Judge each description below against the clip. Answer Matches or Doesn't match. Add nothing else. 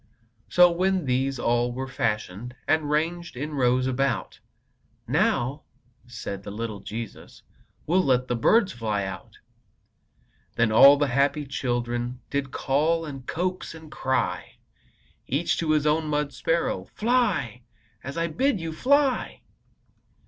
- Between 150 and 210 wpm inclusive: Doesn't match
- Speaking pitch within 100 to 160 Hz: Matches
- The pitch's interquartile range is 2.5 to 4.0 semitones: Doesn't match